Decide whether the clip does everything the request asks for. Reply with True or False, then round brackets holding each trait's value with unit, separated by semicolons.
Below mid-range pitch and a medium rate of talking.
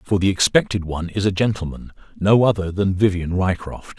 True (95 Hz; 180 wpm)